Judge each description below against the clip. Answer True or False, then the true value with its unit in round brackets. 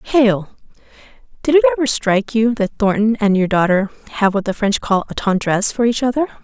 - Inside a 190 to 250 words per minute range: True (195 wpm)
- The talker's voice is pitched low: False (215 Hz)